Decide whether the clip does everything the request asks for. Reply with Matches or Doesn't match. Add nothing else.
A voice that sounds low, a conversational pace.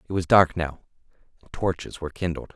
Matches